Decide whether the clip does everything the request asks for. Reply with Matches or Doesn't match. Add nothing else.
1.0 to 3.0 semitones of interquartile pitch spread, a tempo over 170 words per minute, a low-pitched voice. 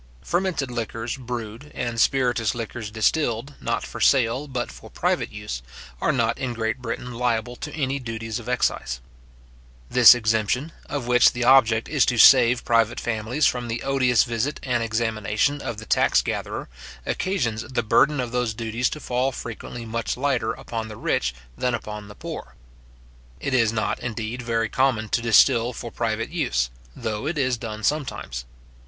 Doesn't match